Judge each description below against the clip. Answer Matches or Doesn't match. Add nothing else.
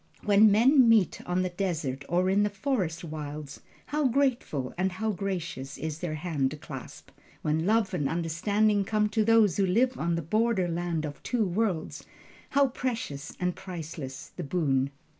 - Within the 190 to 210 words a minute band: Doesn't match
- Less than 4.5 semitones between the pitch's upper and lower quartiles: Doesn't match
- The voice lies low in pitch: Doesn't match